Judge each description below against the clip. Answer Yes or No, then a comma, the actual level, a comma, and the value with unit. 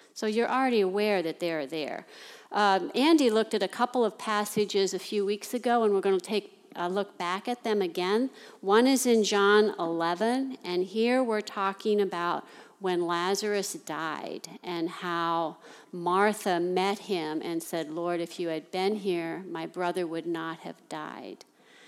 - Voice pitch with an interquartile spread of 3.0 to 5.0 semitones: Yes, average, 3.7 semitones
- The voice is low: No, high, 195 Hz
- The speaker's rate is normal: Yes, average, 170 wpm